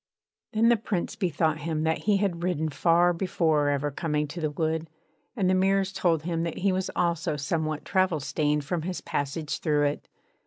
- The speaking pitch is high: No, medium, 165 Hz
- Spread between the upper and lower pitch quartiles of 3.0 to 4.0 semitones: Yes, average, 3.3 semitones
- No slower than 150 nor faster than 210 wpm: Yes, average, 190 wpm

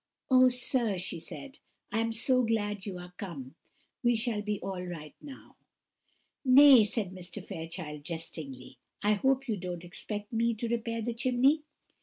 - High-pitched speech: Yes, high, 210 Hz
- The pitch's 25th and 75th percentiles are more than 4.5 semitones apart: Yes, average, 5.2 semitones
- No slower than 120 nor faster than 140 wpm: No, average, 160 wpm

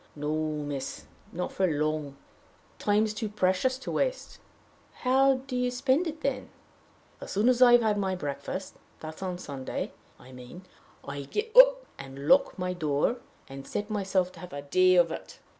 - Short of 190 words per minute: Yes, average, 175 wpm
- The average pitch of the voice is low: No, medium, 185 Hz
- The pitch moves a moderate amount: No, wide, 8.8 semitones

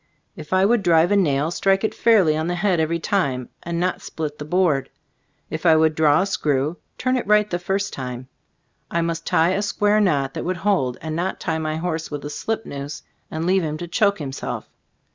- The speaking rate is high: Yes, fast, 220 wpm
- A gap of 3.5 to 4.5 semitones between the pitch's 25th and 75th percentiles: Yes, average, 4.0 semitones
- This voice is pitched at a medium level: Yes, medium, 170 Hz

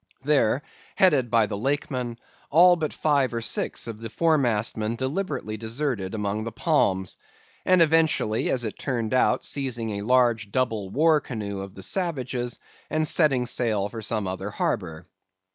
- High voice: No, low, 120 Hz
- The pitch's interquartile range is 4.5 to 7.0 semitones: Yes, average, 5.2 semitones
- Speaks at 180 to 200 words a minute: No, average, 150 wpm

